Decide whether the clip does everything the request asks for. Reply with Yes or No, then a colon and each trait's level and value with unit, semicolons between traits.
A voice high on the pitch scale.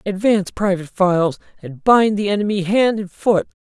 Yes: high, 195 Hz